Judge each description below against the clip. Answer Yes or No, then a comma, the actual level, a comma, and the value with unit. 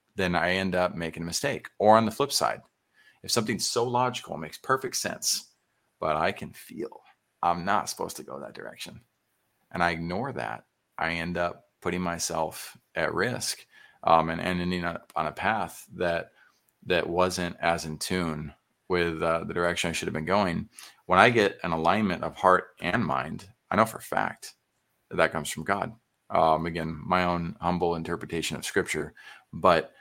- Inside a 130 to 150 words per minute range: No, average, 185 wpm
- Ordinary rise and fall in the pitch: No, narrow, 1.4 semitones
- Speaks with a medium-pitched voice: No, very low, 85 Hz